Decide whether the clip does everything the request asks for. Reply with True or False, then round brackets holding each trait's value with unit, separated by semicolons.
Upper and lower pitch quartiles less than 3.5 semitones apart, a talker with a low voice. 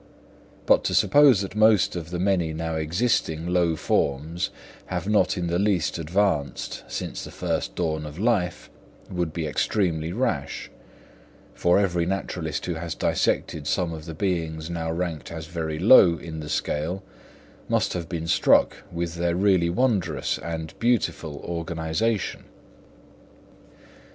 True (2.9 semitones; 85 Hz)